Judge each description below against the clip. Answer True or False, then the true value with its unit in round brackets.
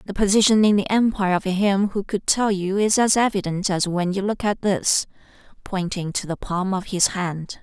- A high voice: True (195 Hz)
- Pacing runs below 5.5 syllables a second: True (4.9 syllables/s)